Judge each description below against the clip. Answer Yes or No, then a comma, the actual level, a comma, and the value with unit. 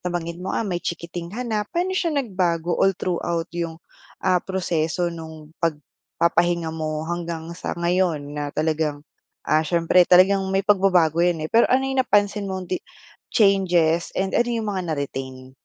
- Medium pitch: Yes, medium, 175 Hz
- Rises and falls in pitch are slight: No, average, 3.1 semitones